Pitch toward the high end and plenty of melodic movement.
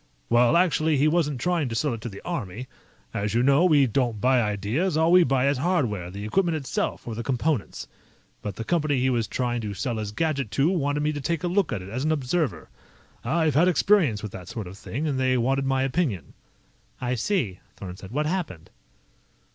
No: low, 130 Hz; wide, 6.0 semitones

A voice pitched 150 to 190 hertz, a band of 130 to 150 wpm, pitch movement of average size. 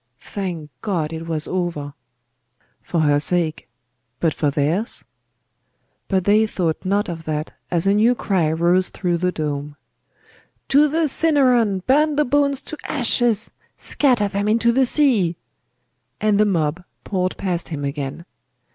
No: medium, 185 Hz; average, 145 wpm; wide, 6.2 semitones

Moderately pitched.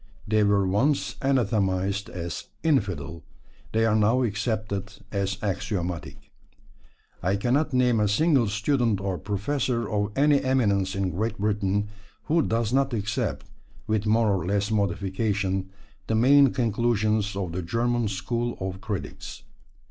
No: low, 105 Hz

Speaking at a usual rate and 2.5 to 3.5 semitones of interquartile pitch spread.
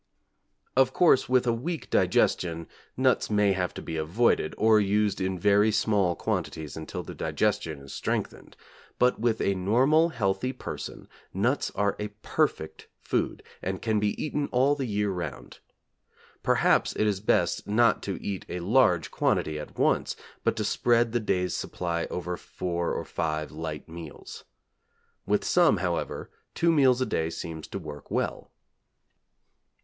No: average, 155 wpm; wide, 5.6 semitones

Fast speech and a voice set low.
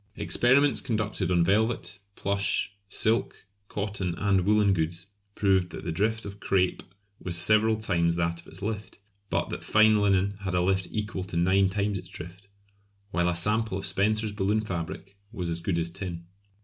No: average, 175 wpm; low, 100 Hz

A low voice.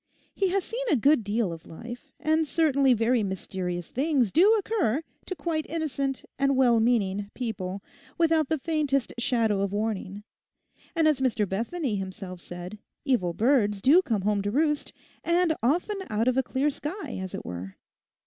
No: very high, 250 Hz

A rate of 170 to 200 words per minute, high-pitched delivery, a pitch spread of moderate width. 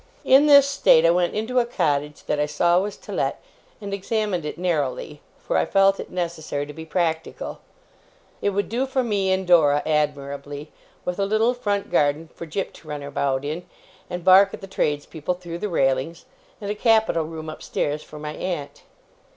No: average, 190 wpm; medium, 170 Hz; average, 5.0 semitones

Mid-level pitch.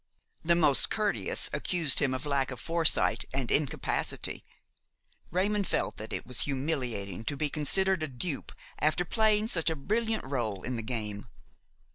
Yes: medium, 150 Hz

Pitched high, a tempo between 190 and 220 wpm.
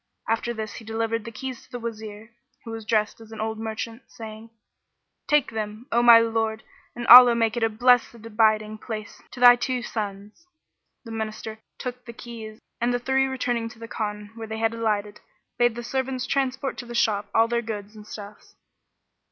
Yes: high, 225 Hz; average, 195 wpm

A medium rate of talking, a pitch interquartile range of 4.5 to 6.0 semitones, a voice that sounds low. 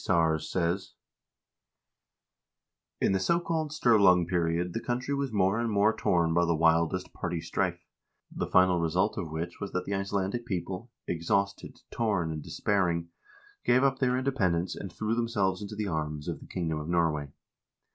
Yes: average, 175 wpm; average, 4.8 semitones; very low, 95 Hz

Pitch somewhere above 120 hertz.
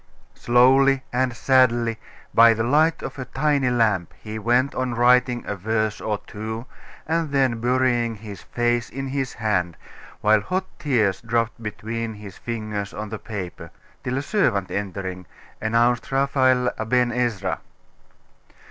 No: low, 115 Hz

